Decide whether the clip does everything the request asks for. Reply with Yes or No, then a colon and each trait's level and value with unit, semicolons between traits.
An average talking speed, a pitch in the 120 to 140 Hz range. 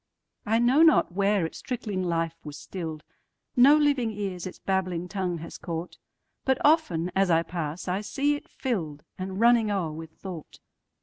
No: average, 150 wpm; high, 190 Hz